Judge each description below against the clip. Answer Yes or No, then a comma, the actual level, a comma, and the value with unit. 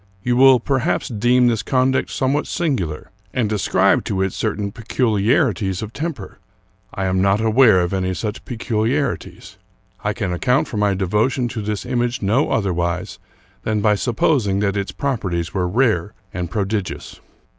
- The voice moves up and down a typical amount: Yes, average, 4.5 semitones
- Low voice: Yes, low, 105 Hz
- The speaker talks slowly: No, average, 155 wpm